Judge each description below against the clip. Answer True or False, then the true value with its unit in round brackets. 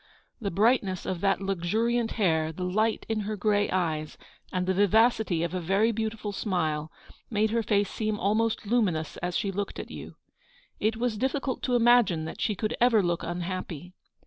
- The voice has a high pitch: True (205 Hz)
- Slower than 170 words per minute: False (180 wpm)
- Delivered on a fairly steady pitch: False (3.8 semitones)